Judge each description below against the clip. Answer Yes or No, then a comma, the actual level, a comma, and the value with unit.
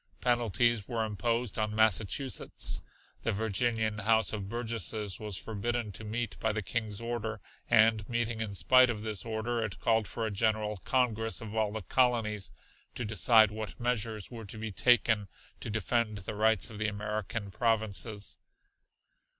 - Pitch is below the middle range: Yes, low, 110 Hz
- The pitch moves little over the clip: Yes, narrow, 1.8 semitones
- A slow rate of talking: No, average, 160 wpm